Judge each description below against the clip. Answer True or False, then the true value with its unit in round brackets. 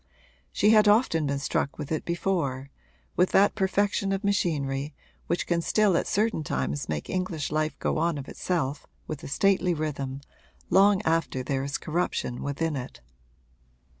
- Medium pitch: True (160 Hz)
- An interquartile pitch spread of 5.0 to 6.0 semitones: True (5.3 semitones)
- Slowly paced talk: False (160 wpm)